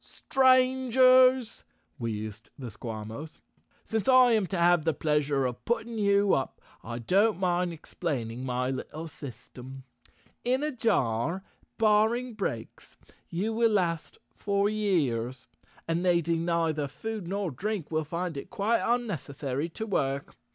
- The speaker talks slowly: Yes, slow, 130 wpm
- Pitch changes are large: Yes, wide, 8.1 semitones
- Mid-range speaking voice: Yes, medium, 170 Hz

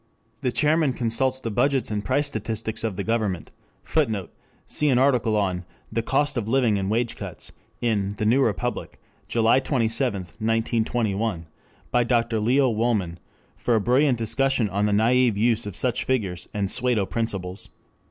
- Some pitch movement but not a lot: Yes, average, 3.5 semitones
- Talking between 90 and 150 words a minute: No, average, 160 wpm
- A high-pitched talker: No, low, 115 Hz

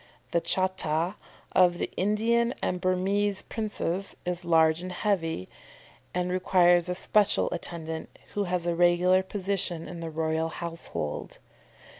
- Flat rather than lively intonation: Yes, narrow, 2.2 semitones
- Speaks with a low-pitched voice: No, medium, 180 Hz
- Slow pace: Yes, slow, 130 wpm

